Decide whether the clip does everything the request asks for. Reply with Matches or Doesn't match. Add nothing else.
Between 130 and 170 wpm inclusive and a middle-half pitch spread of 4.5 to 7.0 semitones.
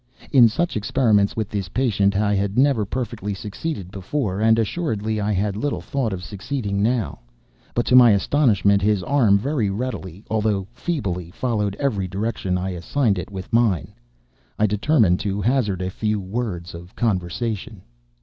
Doesn't match